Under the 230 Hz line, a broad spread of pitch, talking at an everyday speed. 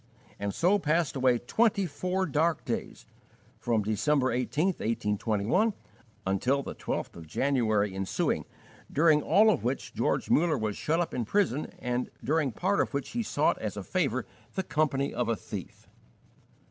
Yes: medium, 140 Hz; wide, 7.1 semitones; average, 160 wpm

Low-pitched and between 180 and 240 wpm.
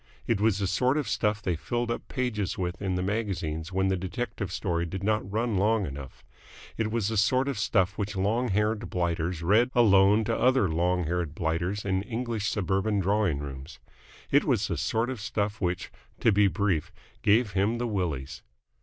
Yes: low, 100 Hz; average, 190 wpm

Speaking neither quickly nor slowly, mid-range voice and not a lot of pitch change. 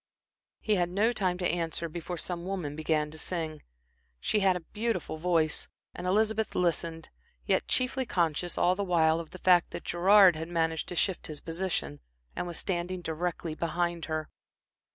Yes: average, 175 wpm; medium, 175 Hz; narrow, 2.3 semitones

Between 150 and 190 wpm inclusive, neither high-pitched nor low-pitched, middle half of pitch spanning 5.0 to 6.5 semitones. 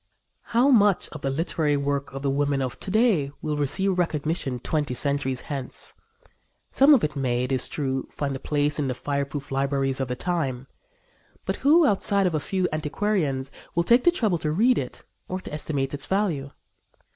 Yes: average, 185 wpm; medium, 145 Hz; average, 5.3 semitones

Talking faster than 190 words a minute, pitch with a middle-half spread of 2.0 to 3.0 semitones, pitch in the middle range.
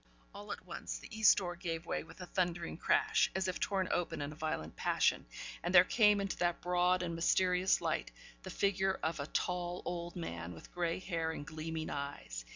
Yes: average, 200 wpm; narrow, 2.5 semitones; medium, 175 Hz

